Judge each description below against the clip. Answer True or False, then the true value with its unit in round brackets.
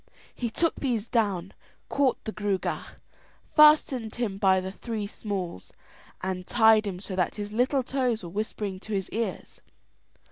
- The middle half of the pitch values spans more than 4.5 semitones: False (3.8 semitones)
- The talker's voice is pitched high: True (215 Hz)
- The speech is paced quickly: False (150 wpm)